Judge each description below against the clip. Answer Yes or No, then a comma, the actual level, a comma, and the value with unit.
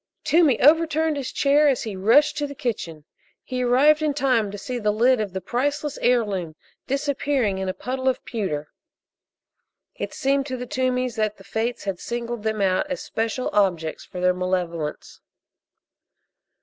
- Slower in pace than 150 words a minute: No, average, 165 wpm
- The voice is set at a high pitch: Yes, high, 240 Hz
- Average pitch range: No, wide, 5.9 semitones